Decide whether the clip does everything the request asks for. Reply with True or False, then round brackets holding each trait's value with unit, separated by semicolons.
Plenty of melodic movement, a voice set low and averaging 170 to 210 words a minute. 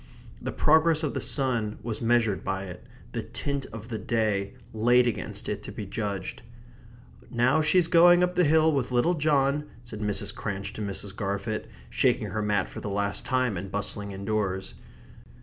True (5.7 semitones; 110 Hz; 175 wpm)